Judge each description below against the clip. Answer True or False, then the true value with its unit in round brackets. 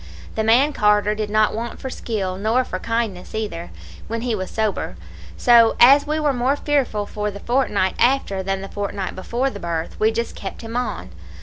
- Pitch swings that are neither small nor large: True (3.5 semitones)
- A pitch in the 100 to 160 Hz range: False (220 Hz)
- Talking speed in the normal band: True (195 wpm)